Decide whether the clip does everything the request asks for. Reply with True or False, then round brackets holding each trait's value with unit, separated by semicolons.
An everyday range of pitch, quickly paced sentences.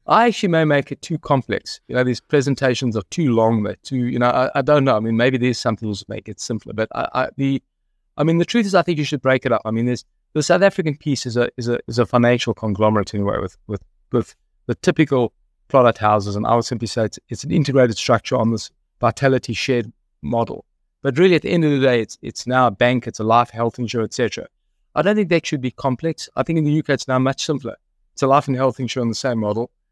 True (3.6 semitones; 260 wpm)